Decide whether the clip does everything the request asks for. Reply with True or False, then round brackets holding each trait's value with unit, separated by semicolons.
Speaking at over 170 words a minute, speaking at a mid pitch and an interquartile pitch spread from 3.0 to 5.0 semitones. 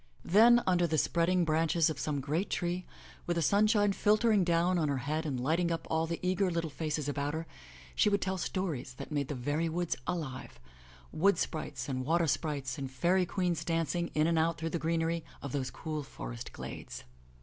True (205 wpm; 165 Hz; 3.4 semitones)